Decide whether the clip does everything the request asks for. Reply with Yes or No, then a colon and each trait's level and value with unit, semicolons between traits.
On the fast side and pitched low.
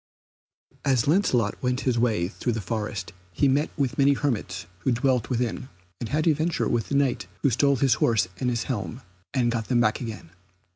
No: average, 190 wpm; low, 125 Hz